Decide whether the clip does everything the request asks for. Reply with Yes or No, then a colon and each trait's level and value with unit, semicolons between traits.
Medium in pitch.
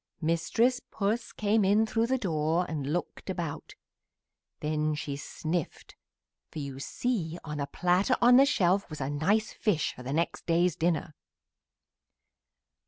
Yes: medium, 170 Hz